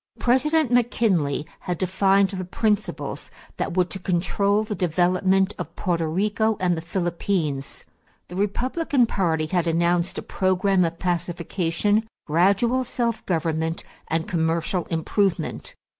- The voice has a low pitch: No, medium, 185 Hz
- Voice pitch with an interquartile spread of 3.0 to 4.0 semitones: Yes, average, 3.5 semitones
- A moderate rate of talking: No, slow, 125 wpm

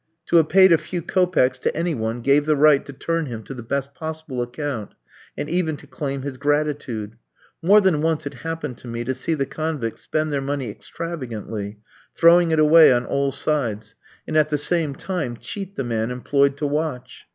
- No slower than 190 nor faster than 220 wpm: Yes, average, 200 wpm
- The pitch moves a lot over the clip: No, average, 4.2 semitones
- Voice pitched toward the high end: No, medium, 145 Hz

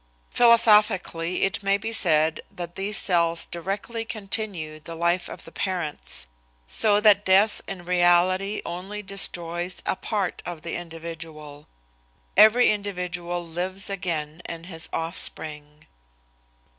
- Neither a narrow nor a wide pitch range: Yes, average, 3.3 semitones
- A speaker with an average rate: No, slow, 120 wpm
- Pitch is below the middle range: No, medium, 175 Hz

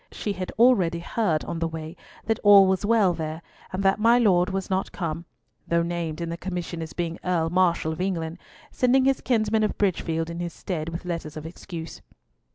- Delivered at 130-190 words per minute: No, average, 200 wpm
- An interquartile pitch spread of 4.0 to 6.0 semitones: No, average, 3.2 semitones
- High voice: No, medium, 175 Hz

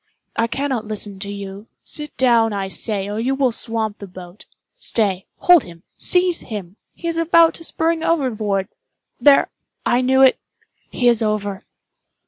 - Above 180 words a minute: No, slow, 135 wpm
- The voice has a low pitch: No, high, 225 Hz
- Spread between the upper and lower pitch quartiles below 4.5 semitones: No, average, 5.2 semitones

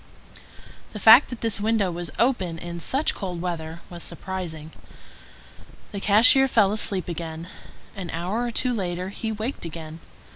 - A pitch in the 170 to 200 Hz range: Yes, high, 190 Hz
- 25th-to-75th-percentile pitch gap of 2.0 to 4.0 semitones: No, average, 4.6 semitones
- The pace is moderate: Yes, average, 150 wpm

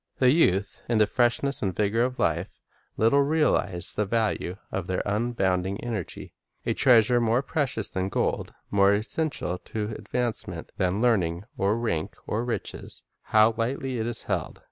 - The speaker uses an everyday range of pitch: Yes, average, 3.9 semitones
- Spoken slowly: No, average, 160 wpm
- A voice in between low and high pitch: No, low, 110 Hz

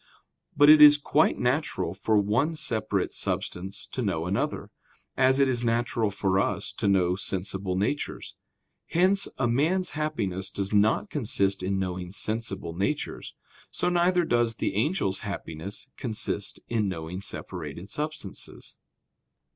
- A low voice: Yes, low, 110 Hz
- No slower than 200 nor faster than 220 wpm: No, slow, 135 wpm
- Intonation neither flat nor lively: No, wide, 7.1 semitones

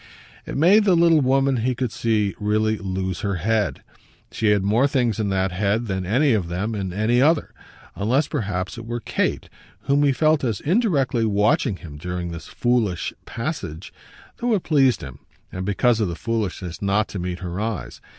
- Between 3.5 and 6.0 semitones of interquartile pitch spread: Yes, wide, 5.5 semitones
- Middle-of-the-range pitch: No, low, 110 Hz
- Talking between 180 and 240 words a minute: Yes, average, 185 wpm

